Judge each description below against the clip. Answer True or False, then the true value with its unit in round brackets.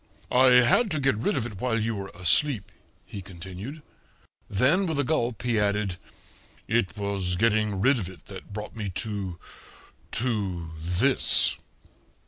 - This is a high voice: False (110 Hz)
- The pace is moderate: True (150 wpm)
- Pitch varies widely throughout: False (4.5 semitones)